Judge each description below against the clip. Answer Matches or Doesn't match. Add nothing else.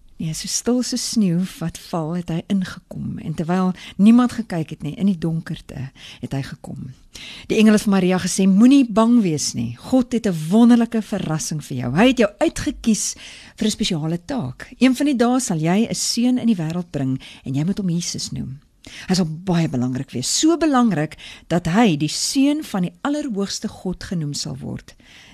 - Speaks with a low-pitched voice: Doesn't match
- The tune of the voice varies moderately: Doesn't match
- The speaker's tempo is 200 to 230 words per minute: Matches